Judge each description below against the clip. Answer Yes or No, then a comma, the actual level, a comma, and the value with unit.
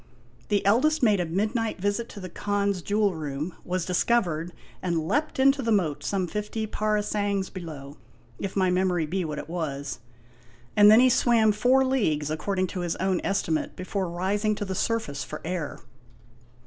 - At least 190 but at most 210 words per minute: No, average, 170 wpm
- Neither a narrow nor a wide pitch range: Yes, average, 3.8 semitones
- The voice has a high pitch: Yes, high, 195 Hz